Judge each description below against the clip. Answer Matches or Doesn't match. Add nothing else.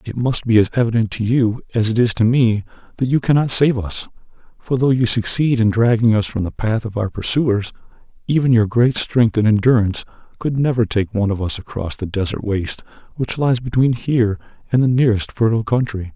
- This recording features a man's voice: Matches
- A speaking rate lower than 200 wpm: Doesn't match